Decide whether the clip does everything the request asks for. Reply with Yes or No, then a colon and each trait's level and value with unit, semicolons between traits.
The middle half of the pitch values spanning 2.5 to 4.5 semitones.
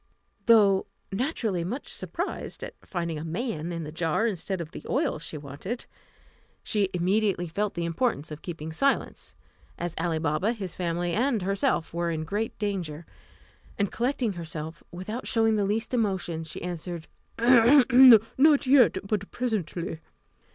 No: average, 5.3 semitones